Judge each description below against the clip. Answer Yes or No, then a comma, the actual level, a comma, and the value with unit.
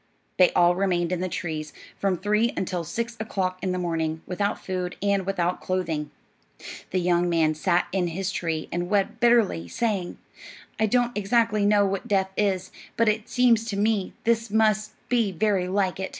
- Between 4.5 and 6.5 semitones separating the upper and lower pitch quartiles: No, average, 3.2 semitones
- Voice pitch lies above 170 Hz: Yes, high, 190 Hz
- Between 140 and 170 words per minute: No, average, 180 wpm